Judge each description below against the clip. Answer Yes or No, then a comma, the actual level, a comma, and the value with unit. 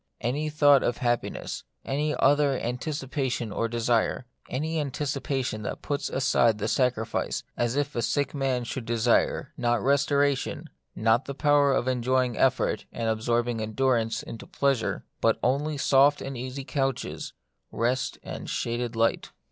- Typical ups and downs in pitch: Yes, average, 3.0 semitones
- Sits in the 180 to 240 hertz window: No, low, 130 Hz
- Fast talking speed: No, average, 155 wpm